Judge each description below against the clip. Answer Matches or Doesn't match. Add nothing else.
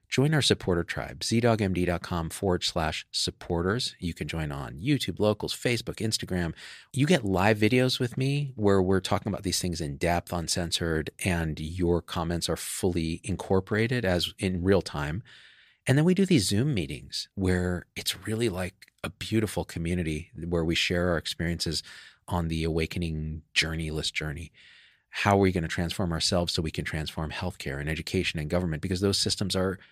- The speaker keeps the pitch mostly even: Doesn't match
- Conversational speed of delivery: Matches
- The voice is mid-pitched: Doesn't match